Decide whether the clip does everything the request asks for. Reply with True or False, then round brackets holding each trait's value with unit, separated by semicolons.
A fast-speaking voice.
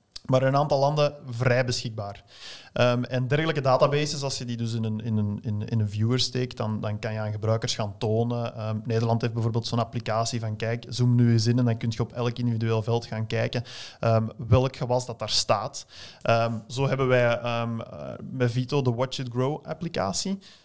True (205 wpm)